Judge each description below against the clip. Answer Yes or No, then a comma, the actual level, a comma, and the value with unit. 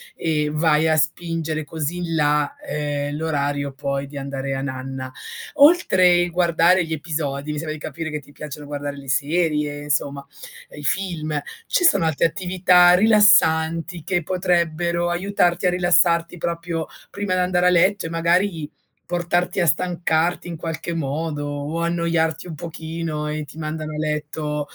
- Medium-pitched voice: Yes, medium, 160 Hz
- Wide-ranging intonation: No, average, 2.8 semitones